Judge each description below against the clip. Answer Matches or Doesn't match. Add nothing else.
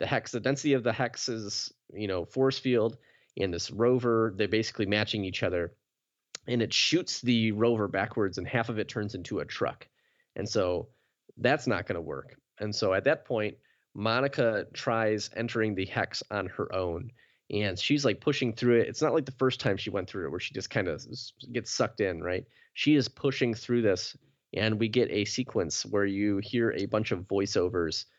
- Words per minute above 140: Matches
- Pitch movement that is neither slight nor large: Matches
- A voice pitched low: Matches